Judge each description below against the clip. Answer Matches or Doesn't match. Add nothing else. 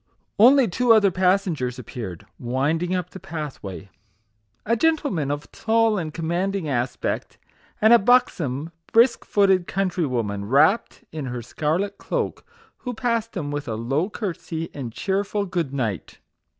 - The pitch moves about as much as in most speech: Doesn't match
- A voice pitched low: Doesn't match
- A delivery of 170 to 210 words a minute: Doesn't match